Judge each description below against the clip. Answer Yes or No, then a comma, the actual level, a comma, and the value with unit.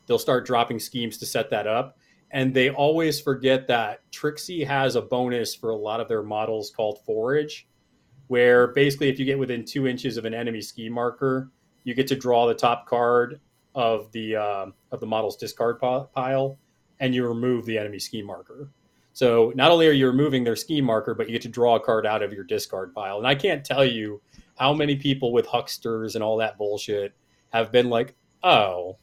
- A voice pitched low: Yes, low, 125 Hz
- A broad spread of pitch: No, average, 3.1 semitones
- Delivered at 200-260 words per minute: Yes, fast, 205 wpm